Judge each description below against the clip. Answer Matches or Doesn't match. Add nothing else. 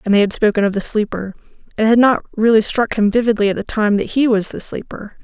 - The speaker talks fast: Matches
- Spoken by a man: Doesn't match